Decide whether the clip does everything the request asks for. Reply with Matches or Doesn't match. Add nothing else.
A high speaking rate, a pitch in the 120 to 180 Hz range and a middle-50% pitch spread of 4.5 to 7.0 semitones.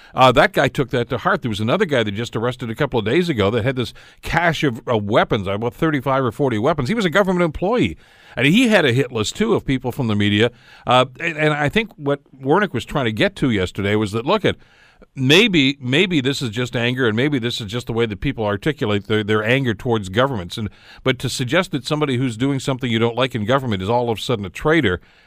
Doesn't match